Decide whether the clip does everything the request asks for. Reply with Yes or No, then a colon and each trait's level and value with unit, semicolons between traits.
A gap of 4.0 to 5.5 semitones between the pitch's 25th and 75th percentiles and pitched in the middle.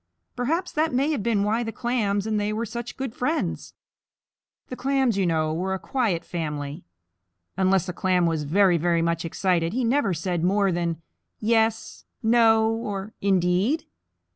No: average, 5.1 semitones; high, 200 Hz